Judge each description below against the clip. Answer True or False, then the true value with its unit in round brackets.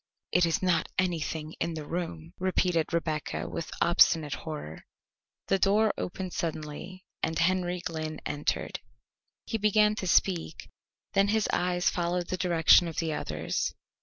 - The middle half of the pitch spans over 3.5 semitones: False (2.6 semitones)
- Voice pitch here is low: False (170 Hz)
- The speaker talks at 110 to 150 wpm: True (140 wpm)